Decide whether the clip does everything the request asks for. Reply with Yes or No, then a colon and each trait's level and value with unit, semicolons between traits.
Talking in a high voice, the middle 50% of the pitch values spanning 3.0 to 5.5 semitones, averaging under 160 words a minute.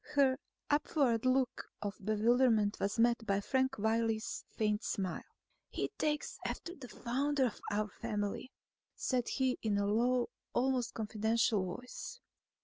Yes: high, 235 Hz; average, 3.6 semitones; slow, 135 wpm